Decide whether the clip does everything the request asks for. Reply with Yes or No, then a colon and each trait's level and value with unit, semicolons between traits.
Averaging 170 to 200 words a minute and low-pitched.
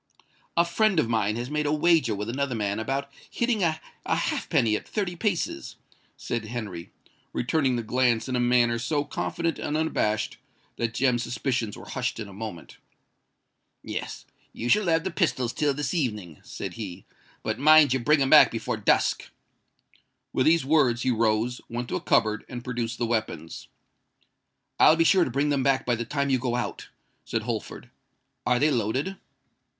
Yes: average, 175 wpm; low, 125 Hz